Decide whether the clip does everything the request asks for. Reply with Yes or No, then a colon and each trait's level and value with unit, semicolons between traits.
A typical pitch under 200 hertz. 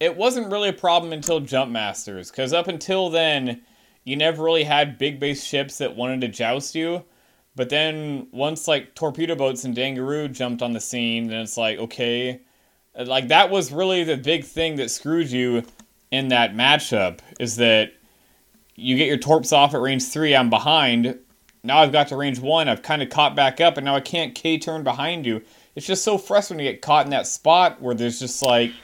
Yes: medium, 140 Hz